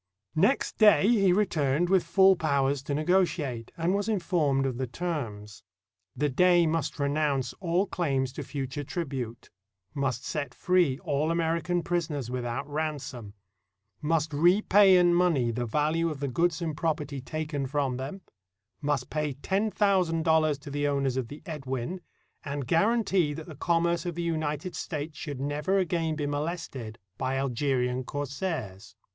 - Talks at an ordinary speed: Yes, average, 150 wpm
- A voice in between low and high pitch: Yes, medium, 150 Hz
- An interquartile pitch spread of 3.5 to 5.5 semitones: Yes, average, 4.2 semitones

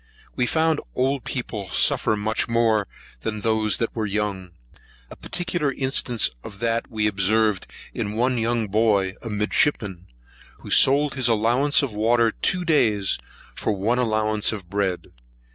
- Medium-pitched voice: No, low, 110 Hz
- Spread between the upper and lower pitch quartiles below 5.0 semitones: Yes, average, 3.0 semitones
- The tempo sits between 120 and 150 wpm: Yes, average, 145 wpm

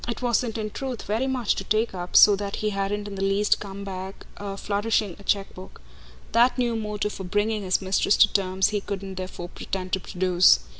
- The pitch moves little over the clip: Yes, narrow, 2.1 semitones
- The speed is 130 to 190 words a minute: No, average, 200 wpm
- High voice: Yes, high, 200 Hz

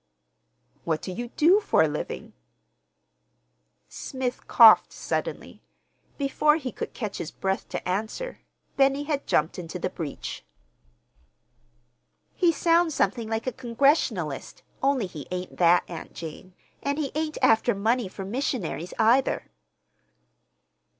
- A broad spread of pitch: Yes, wide, 7.4 semitones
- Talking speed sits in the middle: No, slow, 125 wpm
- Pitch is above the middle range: Yes, high, 230 Hz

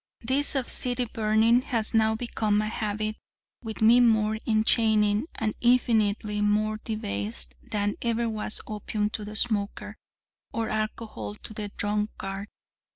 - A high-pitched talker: Yes, high, 215 Hz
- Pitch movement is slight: Yes, narrow, 1.5 semitones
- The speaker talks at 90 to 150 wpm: Yes, slow, 135 wpm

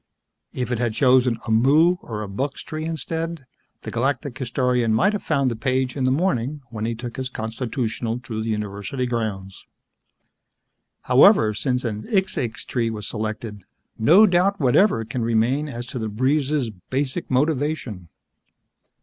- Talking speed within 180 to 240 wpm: No, average, 155 wpm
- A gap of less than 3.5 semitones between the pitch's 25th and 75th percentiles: No, average, 4.2 semitones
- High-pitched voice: No, low, 125 Hz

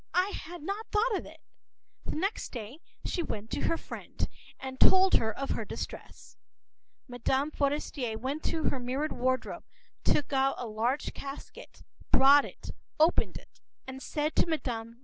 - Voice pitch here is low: No, very high, 275 Hz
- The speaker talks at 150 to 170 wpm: Yes, average, 160 wpm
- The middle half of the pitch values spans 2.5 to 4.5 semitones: Yes, average, 4.2 semitones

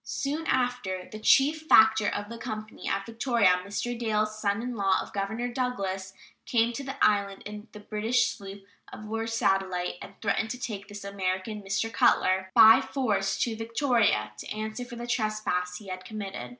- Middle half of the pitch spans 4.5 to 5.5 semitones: No, average, 3.1 semitones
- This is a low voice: No, high, 215 Hz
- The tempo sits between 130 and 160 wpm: No, average, 175 wpm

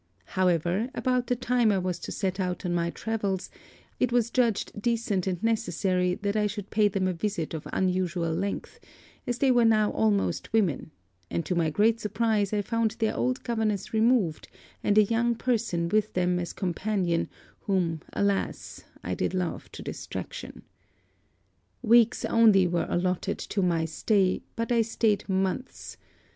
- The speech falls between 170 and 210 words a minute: No, average, 160 wpm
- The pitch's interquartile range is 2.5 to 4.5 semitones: Yes, average, 3.9 semitones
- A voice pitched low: No, high, 200 Hz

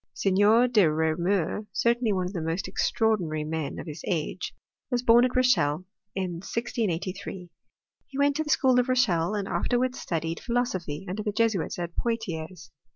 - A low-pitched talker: No, high, 195 Hz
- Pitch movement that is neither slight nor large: No, wide, 6.0 semitones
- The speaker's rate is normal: Yes, average, 165 wpm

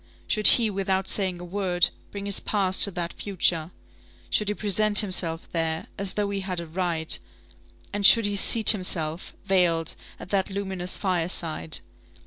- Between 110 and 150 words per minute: No, average, 160 wpm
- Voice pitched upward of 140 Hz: Yes, high, 190 Hz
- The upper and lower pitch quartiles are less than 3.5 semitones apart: Yes, average, 2.8 semitones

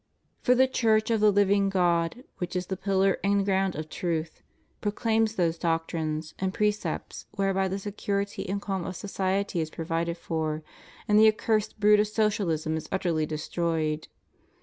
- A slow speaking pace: No, average, 165 wpm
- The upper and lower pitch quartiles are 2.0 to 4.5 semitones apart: Yes, average, 3.8 semitones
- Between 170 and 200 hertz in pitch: Yes, high, 190 Hz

